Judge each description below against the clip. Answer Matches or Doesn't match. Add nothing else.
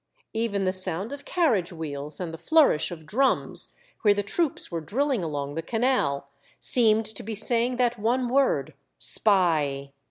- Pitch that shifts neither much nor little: Doesn't match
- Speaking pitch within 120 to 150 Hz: Doesn't match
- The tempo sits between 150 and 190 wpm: Matches